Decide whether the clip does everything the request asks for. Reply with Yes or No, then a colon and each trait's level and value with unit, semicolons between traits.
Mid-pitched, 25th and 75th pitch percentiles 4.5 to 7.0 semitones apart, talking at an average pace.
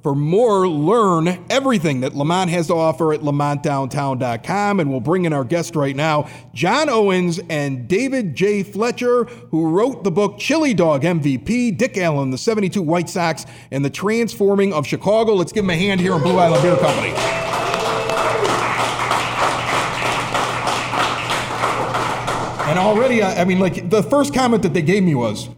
Yes: medium, 175 Hz; average, 5.2 semitones; average, 155 wpm